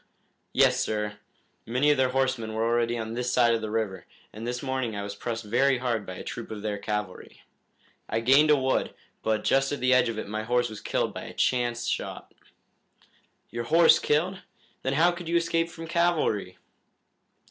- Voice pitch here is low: Yes, low, 120 Hz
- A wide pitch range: No, average, 3.7 semitones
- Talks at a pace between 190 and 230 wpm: Yes, average, 195 wpm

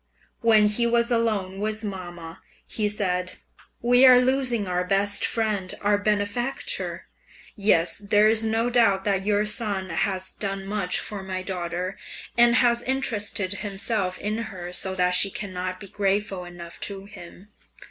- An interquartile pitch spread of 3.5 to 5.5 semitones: No, average, 2.9 semitones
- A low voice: No, high, 205 Hz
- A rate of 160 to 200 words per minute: No, average, 150 wpm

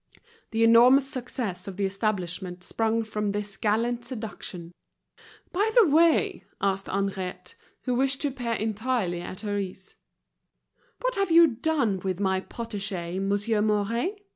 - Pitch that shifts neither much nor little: Yes, average, 4.3 semitones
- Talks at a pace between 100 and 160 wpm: Yes, average, 140 wpm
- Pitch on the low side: No, high, 215 Hz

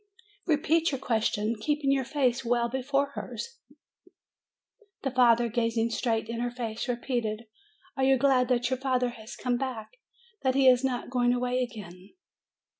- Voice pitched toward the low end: No, high, 245 Hz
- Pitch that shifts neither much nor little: No, narrow, 2.3 semitones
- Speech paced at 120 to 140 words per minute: No, average, 155 wpm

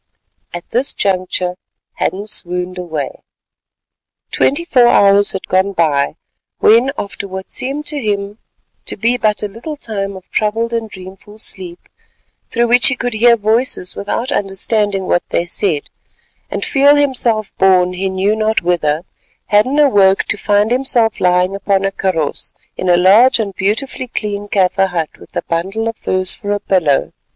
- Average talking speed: Yes, average, 160 wpm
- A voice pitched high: Yes, high, 200 Hz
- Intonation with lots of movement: No, average, 3.6 semitones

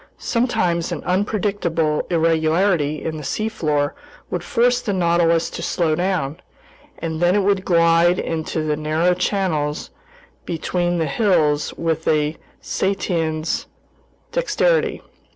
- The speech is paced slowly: Yes, slow, 115 wpm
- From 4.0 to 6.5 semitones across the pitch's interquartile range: No, average, 3.2 semitones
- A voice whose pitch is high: No, medium, 170 Hz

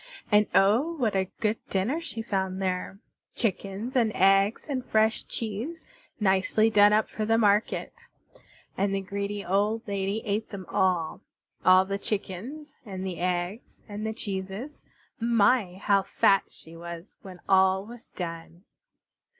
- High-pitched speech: Yes, high, 200 Hz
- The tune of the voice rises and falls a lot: No, average, 2.7 semitones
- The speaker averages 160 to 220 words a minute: No, average, 145 wpm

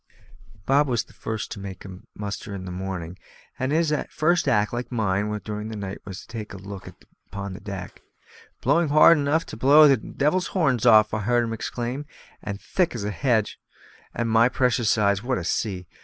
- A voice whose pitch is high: No, low, 110 Hz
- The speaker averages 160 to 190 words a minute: No, average, 200 wpm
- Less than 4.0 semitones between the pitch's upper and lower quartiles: No, average, 4.9 semitones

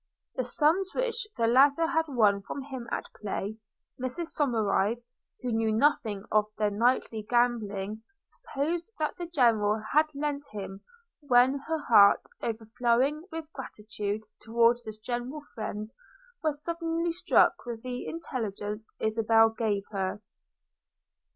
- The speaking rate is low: Yes, slow, 130 wpm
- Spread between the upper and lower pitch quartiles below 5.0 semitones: No, average, 5.3 semitones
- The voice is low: No, high, 240 Hz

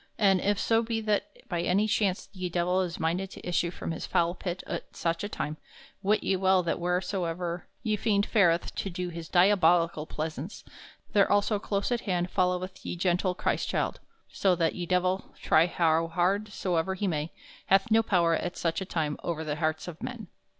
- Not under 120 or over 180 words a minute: No, average, 190 wpm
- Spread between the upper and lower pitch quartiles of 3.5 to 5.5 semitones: No, average, 2.7 semitones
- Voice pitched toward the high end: No, medium, 180 Hz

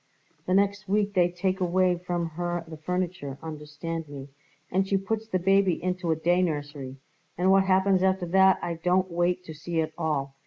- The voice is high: No, medium, 175 Hz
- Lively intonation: No, average, 2.8 semitones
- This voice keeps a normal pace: Yes, average, 190 wpm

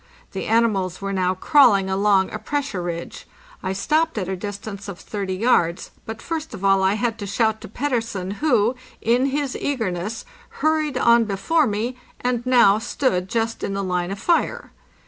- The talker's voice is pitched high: Yes, high, 215 Hz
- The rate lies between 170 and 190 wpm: Yes, average, 180 wpm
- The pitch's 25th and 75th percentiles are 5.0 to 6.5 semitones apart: No, average, 4.6 semitones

